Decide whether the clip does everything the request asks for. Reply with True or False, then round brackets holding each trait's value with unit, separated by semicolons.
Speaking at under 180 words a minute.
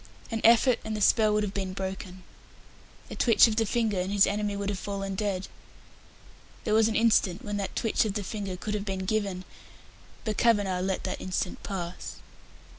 False (190 wpm)